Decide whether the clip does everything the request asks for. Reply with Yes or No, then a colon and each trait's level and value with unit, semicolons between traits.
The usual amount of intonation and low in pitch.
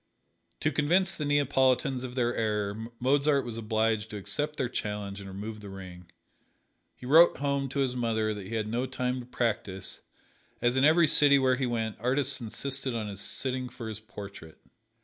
Yes: average, 4.3 semitones; low, 120 Hz